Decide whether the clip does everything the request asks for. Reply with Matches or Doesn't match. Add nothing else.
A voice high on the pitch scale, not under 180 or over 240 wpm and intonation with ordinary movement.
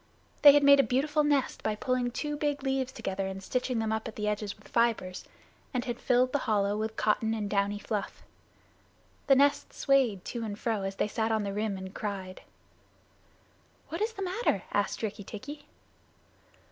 Matches